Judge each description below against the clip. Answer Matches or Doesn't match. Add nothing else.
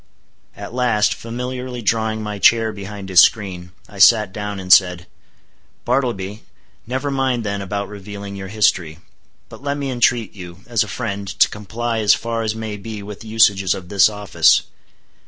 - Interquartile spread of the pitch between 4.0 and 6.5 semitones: Doesn't match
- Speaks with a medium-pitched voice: Doesn't match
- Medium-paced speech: Matches